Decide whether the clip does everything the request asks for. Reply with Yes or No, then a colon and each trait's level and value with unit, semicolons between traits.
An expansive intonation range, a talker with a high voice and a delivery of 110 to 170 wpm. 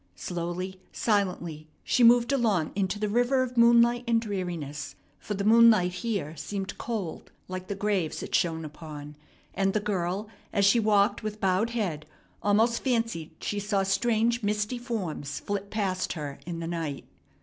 No: average, 4.6 semitones; high, 200 Hz; average, 160 wpm